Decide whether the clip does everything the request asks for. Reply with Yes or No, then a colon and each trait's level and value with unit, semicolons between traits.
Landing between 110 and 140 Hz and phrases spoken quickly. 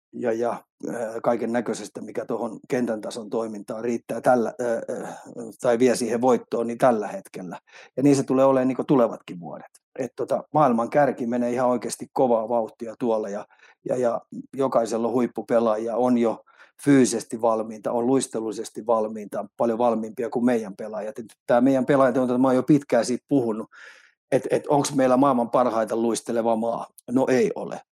Yes: low, 120 Hz; fast, 165 wpm